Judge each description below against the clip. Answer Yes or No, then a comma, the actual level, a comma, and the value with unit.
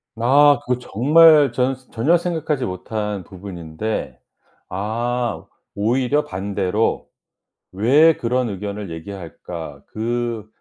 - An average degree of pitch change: Yes, average, 4.9 semitones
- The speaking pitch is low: Yes, low, 110 Hz